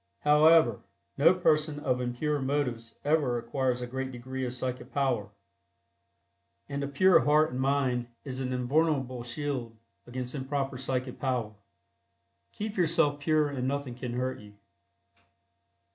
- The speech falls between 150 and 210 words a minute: No, slow, 135 wpm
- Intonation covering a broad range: No, average, 2.9 semitones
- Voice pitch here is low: Yes, low, 130 Hz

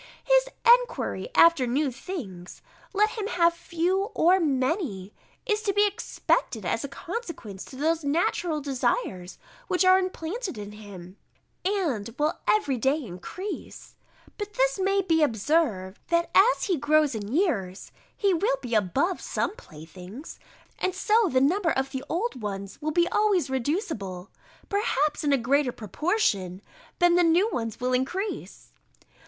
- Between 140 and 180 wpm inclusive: Yes, average, 150 wpm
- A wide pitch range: Yes, wide, 8.6 semitones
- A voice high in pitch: Yes, very high, 310 Hz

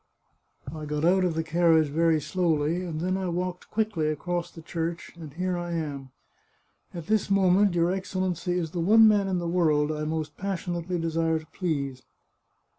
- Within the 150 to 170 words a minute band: No, average, 185 wpm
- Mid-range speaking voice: Yes, medium, 170 Hz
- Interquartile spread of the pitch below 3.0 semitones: Yes, narrow, 2.5 semitones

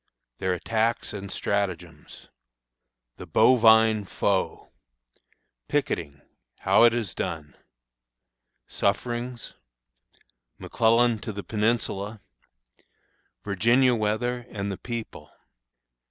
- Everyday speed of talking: No, slow, 80 wpm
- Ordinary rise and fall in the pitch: Yes, average, 3.1 semitones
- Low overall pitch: Yes, low, 110 Hz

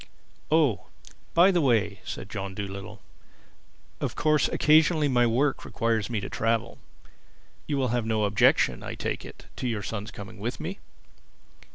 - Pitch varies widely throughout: Yes, wide, 6.1 semitones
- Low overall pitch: Yes, low, 115 Hz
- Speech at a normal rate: Yes, average, 155 wpm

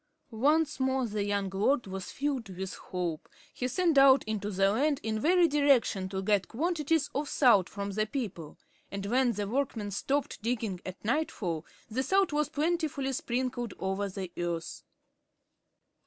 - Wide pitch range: Yes, wide, 6.2 semitones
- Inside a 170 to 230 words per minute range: No, average, 155 wpm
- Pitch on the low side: No, high, 230 Hz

